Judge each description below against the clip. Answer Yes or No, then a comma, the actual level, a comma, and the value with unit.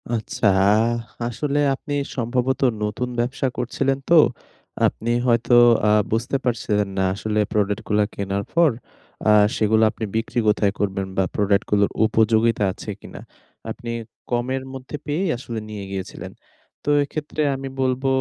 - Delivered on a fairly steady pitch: No, average, 3.9 semitones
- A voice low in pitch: Yes, low, 115 Hz